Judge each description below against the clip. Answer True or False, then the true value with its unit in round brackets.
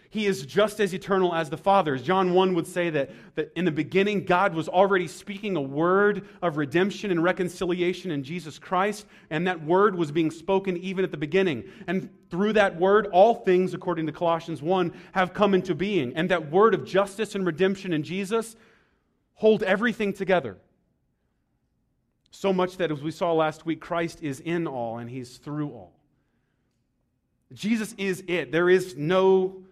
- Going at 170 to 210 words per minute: True (180 wpm)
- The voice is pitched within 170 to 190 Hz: True (185 Hz)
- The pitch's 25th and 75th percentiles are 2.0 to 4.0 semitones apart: True (2.8 semitones)